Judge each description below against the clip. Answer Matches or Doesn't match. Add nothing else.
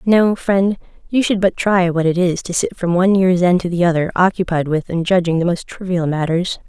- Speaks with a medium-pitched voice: Matches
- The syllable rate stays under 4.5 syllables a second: Doesn't match